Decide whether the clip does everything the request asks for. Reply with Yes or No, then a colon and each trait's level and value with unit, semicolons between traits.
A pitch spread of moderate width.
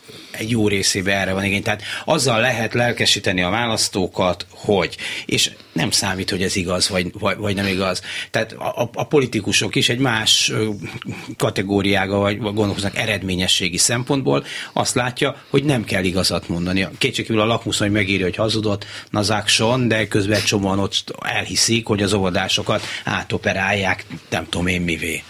Yes: average, 3.0 semitones